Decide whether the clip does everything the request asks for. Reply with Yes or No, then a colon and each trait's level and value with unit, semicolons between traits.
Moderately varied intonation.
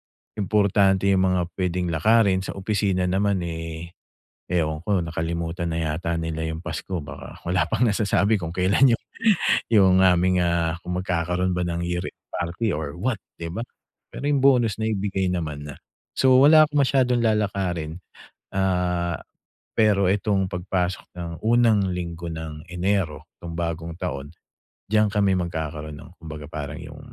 Yes: average, 3.3 semitones